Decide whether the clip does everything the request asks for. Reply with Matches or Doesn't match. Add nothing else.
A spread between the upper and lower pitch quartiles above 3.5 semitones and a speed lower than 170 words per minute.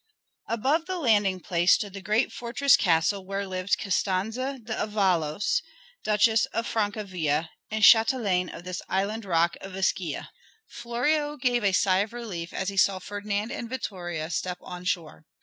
Matches